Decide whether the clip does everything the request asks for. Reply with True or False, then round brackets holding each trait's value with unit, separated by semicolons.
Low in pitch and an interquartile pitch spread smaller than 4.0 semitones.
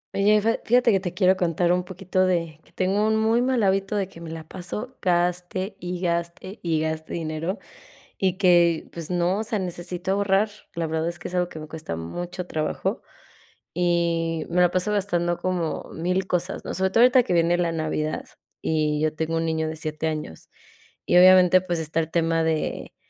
False (175 Hz; 2.5 semitones)